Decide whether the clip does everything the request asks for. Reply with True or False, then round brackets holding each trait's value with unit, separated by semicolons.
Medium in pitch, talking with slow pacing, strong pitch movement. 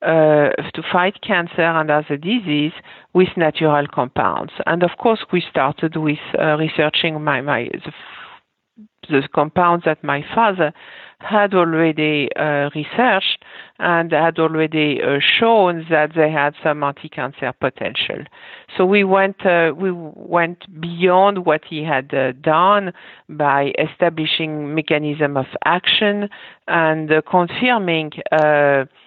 False (160 Hz; 130 wpm; 3.1 semitones)